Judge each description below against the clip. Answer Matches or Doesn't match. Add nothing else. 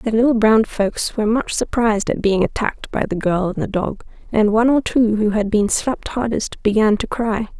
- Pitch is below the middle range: Doesn't match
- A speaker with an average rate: Doesn't match